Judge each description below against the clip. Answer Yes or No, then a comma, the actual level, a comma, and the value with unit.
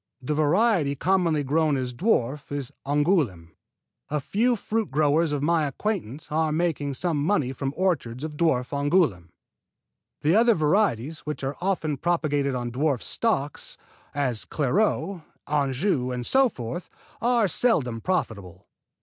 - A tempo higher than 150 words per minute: No, slow, 135 wpm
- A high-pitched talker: No, medium, 150 Hz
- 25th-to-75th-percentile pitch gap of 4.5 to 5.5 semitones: Yes, average, 4.9 semitones